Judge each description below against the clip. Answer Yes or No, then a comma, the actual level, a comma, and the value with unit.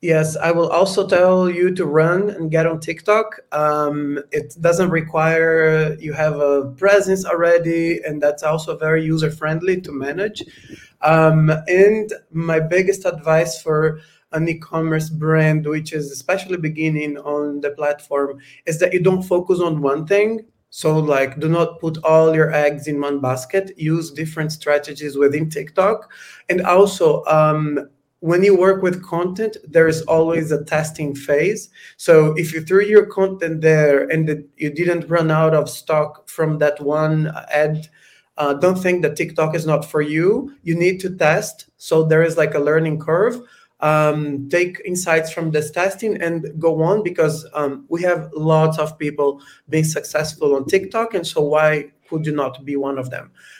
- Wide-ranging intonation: No, narrow, 2.6 semitones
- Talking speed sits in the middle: Yes, average, 170 wpm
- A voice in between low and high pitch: Yes, medium, 160 Hz